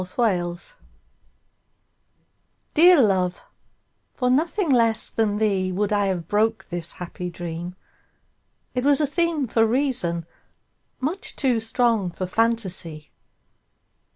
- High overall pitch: Yes, high, 215 Hz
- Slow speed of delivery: Yes, slow, 100 wpm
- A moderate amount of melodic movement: No, wide, 5.8 semitones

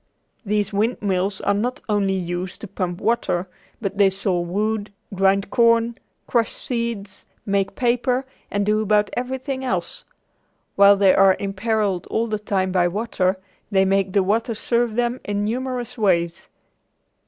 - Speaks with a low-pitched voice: No, high, 205 Hz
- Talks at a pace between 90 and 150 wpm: Yes, average, 145 wpm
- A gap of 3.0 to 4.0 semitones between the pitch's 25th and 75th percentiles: Yes, average, 3.3 semitones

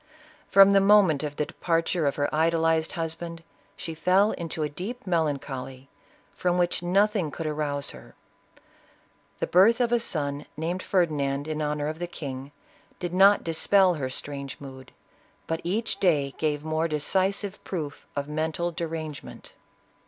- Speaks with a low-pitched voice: No, medium, 160 Hz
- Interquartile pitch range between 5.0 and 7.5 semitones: No, average, 3.7 semitones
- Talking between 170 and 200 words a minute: No, average, 150 wpm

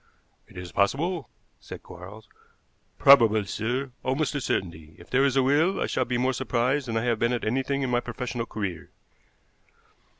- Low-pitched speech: Yes, low, 125 Hz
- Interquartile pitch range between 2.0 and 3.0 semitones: No, average, 3.8 semitones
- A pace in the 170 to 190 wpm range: Yes, average, 175 wpm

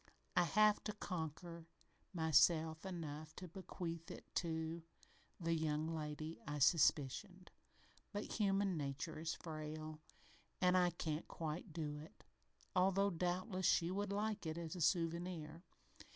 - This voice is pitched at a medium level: Yes, medium, 165 Hz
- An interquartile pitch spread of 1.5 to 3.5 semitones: Yes, average, 2.8 semitones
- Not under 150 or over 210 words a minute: No, slow, 135 wpm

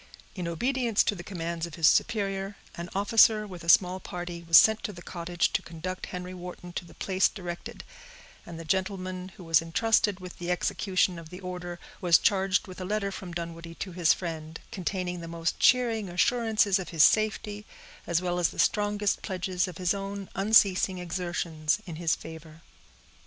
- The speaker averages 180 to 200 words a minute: Yes, average, 185 wpm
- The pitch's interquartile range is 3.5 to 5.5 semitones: No, narrow, 2.6 semitones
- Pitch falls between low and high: Yes, medium, 180 Hz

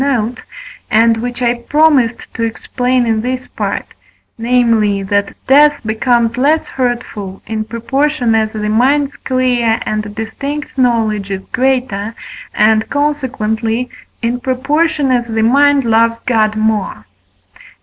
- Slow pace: Yes, slow, 125 wpm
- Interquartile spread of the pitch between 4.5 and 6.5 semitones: No, average, 2.9 semitones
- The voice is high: Yes, high, 235 Hz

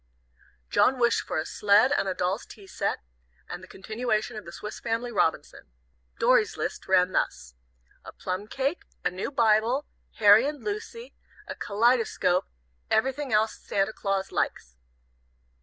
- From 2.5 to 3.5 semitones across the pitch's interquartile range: No, average, 4.6 semitones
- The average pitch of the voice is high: Yes, high, 215 Hz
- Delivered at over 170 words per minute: No, average, 145 wpm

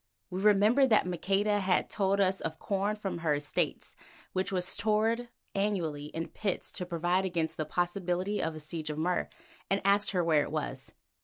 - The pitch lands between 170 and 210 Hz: Yes, medium, 185 Hz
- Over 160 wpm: Yes, average, 180 wpm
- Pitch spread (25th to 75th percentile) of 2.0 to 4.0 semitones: Yes, average, 3.4 semitones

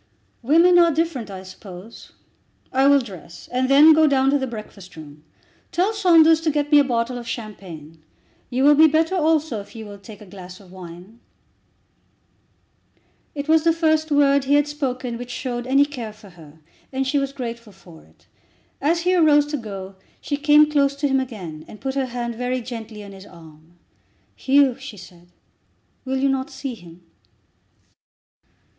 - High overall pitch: Yes, very high, 255 Hz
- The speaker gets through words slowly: No, average, 180 wpm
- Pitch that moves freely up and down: Yes, wide, 6.4 semitones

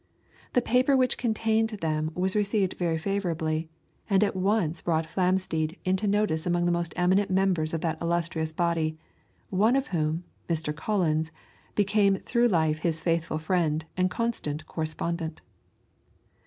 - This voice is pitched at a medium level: Yes, medium, 175 Hz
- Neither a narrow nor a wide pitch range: Yes, average, 3.9 semitones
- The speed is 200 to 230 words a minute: No, average, 140 wpm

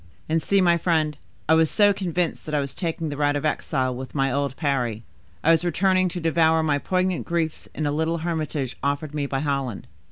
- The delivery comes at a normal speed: No, fast, 215 wpm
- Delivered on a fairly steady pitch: No, average, 3.1 semitones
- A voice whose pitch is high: No, medium, 155 Hz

